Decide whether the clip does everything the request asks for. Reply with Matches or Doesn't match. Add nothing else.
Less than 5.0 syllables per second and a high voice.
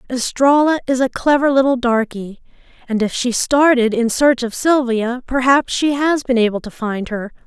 Matches